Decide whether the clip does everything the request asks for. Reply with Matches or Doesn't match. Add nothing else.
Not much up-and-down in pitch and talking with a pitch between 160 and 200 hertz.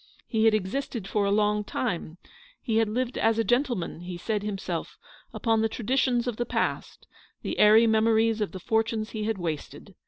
Doesn't match